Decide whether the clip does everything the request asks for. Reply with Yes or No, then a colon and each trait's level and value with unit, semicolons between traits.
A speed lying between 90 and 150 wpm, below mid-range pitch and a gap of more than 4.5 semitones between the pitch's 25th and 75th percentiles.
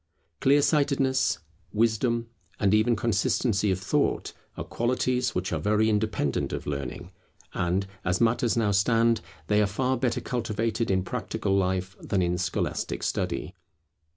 No: average, 140 wpm; low, 110 Hz; average, 3.9 semitones